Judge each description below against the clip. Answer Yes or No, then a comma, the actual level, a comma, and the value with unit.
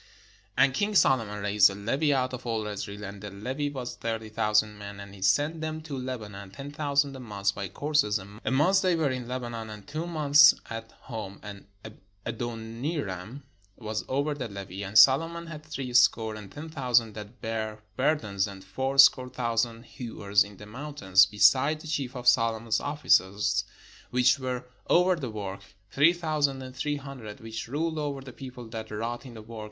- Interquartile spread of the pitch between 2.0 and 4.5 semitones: No, average, 5.2 semitones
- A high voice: No, low, 120 Hz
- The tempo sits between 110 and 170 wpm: No, average, 185 wpm